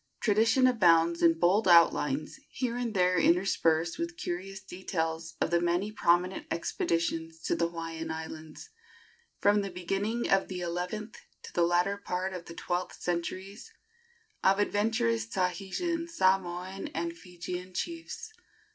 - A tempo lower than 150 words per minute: Yes, slow, 135 wpm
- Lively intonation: No, average, 3.1 semitones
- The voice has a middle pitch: Yes, medium, 180 Hz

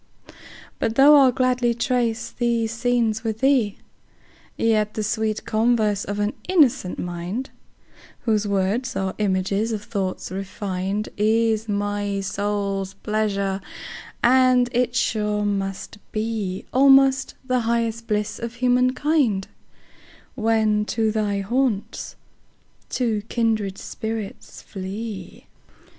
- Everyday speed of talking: No, slow, 100 wpm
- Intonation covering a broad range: No, average, 2.8 semitones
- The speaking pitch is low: No, high, 220 Hz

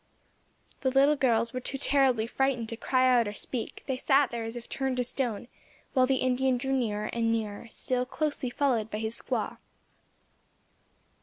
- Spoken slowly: No, average, 175 wpm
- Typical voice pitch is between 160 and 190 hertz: No, very high, 250 Hz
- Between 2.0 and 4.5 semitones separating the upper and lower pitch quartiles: Yes, average, 2.7 semitones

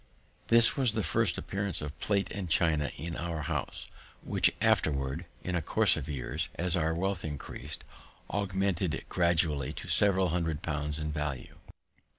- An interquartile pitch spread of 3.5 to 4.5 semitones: Yes, average, 3.9 semitones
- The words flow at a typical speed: Yes, average, 155 wpm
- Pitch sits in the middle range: No, very low, 85 Hz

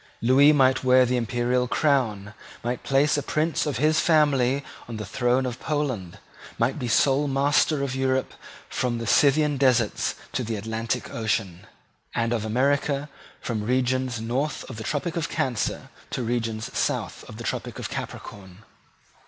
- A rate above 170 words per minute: No, average, 160 wpm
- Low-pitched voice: Yes, low, 125 Hz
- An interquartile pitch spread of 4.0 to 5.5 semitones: No, average, 3.4 semitones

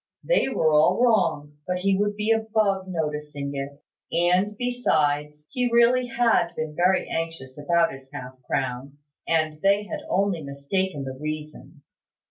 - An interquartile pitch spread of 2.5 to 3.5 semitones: No, wide, 5.6 semitones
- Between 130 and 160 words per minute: Yes, average, 145 wpm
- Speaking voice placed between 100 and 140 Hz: No, medium, 165 Hz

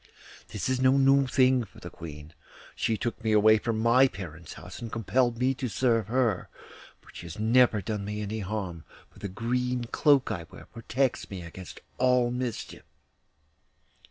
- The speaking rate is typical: Yes, average, 175 wpm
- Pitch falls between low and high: No, low, 115 Hz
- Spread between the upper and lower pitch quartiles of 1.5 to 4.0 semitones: Yes, average, 3.7 semitones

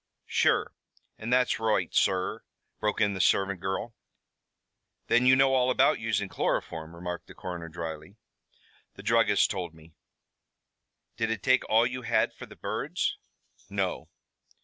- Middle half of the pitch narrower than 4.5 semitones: No, average, 4.9 semitones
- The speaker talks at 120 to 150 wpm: Yes, average, 145 wpm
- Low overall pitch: Yes, low, 105 Hz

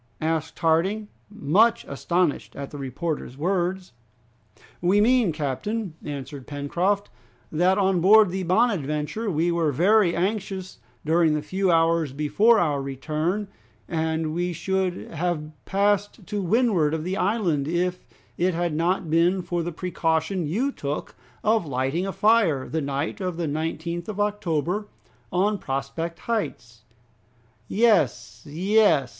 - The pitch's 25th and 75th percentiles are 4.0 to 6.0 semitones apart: Yes, average, 4.3 semitones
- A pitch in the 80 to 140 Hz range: No, medium, 175 Hz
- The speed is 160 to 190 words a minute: No, slow, 135 wpm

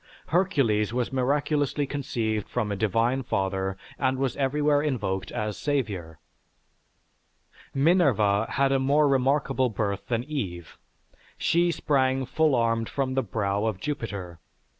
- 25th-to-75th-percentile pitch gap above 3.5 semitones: Yes, average, 5.2 semitones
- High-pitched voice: No, low, 125 Hz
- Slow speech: Yes, slow, 125 wpm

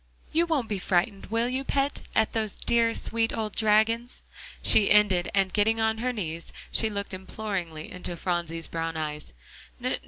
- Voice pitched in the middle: No, high, 210 Hz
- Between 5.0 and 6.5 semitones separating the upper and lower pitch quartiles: No, average, 4.2 semitones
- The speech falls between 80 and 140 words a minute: No, average, 160 wpm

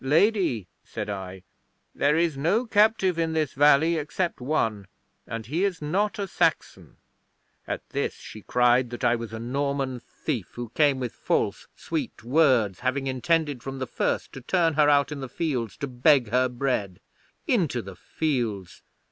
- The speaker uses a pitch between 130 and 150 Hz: Yes, low, 135 Hz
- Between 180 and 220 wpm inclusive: No, average, 165 wpm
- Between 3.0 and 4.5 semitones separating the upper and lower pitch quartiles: No, average, 4.9 semitones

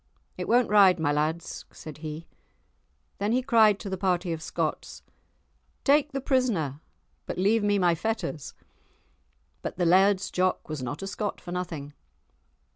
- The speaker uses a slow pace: No, average, 155 wpm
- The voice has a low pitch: No, medium, 185 Hz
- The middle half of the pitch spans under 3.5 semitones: No, average, 4.7 semitones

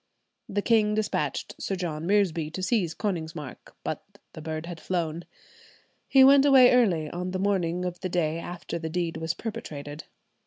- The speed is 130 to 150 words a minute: No, average, 165 wpm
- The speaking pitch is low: No, medium, 175 Hz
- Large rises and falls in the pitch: No, average, 4.1 semitones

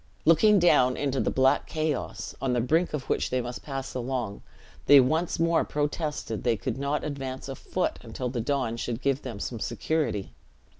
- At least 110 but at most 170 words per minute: No, average, 185 wpm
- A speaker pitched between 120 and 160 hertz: Yes, low, 135 Hz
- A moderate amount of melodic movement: Yes, average, 3.6 semitones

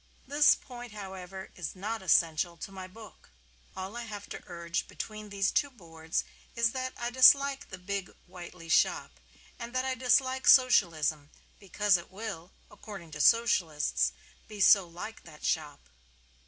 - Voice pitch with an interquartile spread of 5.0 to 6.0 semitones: Yes, wide, 5.4 semitones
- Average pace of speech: Yes, average, 155 wpm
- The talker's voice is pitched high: Yes, high, 195 Hz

